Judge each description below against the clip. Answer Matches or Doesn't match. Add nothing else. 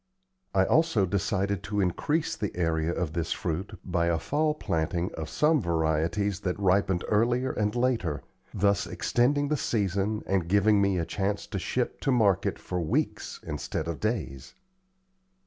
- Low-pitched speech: Matches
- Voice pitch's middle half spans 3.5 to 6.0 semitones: Matches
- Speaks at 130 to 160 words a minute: Matches